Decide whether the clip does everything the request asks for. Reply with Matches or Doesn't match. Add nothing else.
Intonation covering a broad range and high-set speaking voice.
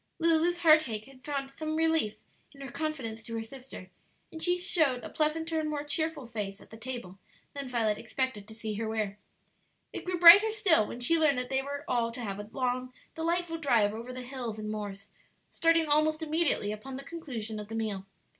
Matches